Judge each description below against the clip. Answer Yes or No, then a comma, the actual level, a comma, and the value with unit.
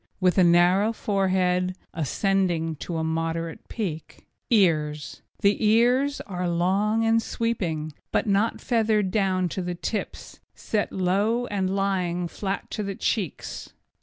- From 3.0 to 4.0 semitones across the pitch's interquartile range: Yes, average, 3.4 semitones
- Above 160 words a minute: No, slow, 135 wpm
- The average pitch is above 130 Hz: Yes, high, 190 Hz